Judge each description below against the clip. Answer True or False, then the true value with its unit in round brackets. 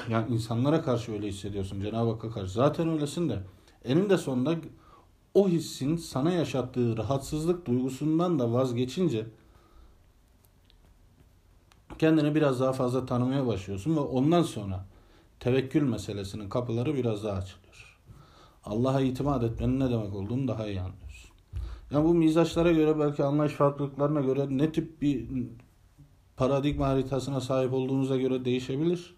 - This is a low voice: True (130 Hz)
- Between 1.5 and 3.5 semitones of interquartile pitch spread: False (5.5 semitones)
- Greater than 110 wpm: True (125 wpm)